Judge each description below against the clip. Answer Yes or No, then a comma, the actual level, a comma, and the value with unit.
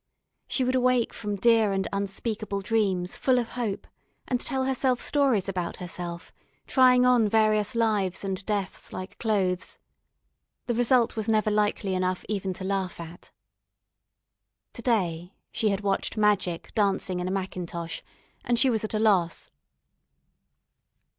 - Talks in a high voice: Yes, high, 205 Hz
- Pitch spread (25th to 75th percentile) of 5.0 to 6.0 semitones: No, average, 3.6 semitones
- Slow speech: No, average, 145 wpm